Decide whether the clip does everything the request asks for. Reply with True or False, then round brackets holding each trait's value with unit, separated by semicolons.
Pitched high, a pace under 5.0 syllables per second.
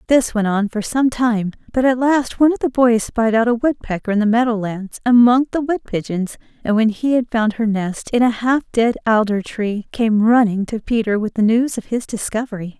False (230 Hz; 5.1 syllables/s)